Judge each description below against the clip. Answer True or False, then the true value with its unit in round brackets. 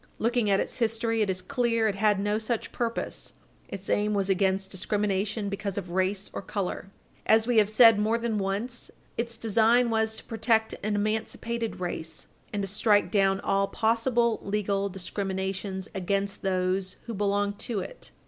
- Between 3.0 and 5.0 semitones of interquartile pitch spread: False (2.5 semitones)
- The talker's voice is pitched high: True (205 Hz)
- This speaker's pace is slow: False (165 wpm)